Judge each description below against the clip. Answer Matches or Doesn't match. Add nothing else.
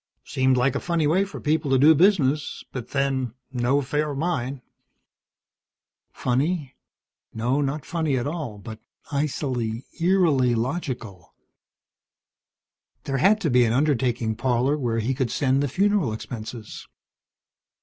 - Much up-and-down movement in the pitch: Doesn't match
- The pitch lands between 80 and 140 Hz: Matches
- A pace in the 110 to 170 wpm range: Matches